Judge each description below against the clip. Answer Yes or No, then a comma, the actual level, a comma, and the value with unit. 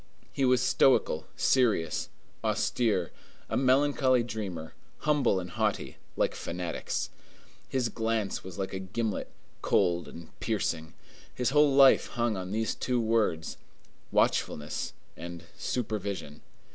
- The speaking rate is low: Yes, slow, 120 wpm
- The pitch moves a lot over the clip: Yes, wide, 6.0 semitones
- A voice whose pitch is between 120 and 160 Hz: No, low, 110 Hz